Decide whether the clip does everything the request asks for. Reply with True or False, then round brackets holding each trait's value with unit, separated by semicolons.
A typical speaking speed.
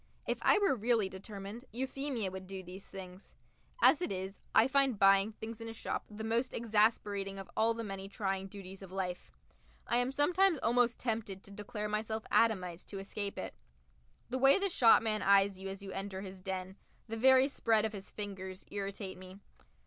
True (185 wpm)